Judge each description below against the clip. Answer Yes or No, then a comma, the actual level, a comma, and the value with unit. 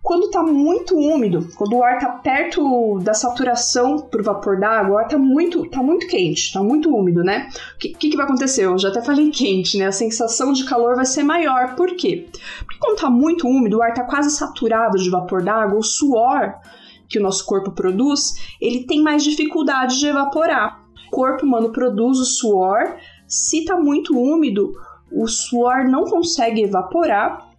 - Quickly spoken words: Yes, fast, 190 wpm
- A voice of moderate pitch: No, very high, 260 Hz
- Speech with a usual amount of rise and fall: No, wide, 5.7 semitones